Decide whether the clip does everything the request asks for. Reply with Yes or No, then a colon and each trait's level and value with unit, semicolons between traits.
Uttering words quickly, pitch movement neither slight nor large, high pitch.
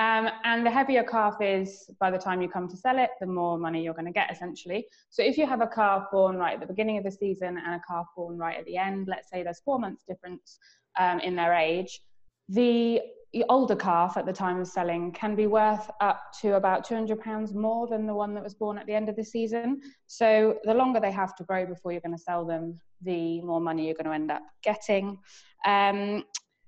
Yes: fast, 235 wpm; average, 3.6 semitones; high, 200 Hz